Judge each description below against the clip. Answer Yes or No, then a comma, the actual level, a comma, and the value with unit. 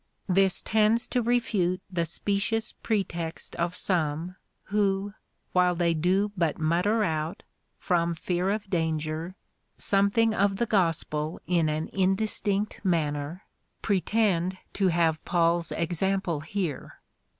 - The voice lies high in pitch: No, medium, 180 Hz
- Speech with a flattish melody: No, average, 3.3 semitones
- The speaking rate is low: Yes, slow, 120 wpm